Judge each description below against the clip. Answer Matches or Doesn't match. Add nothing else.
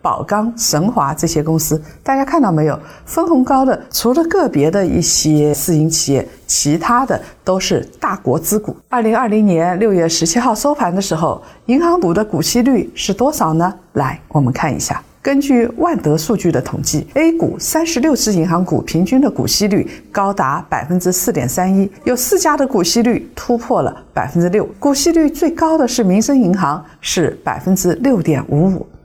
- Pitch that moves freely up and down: Matches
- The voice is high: Matches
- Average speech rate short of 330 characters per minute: Matches